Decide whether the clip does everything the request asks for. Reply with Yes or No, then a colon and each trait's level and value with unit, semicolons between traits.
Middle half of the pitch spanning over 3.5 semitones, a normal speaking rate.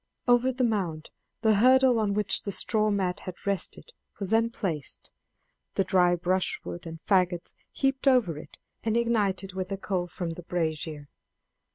Yes: average, 4.2 semitones; average, 160 wpm